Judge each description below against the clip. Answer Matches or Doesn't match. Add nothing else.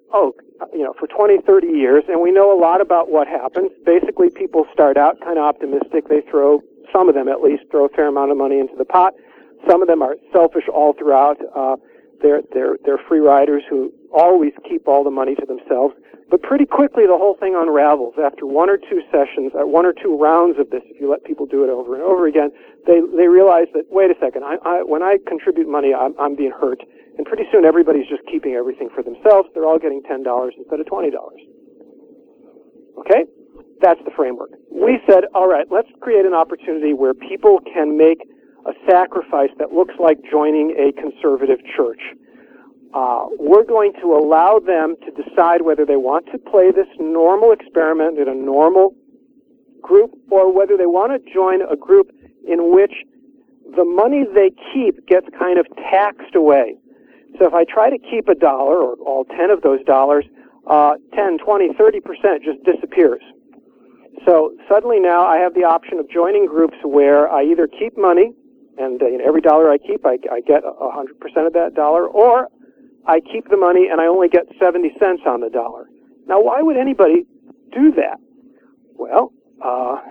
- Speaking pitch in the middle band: Matches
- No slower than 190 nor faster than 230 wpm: Matches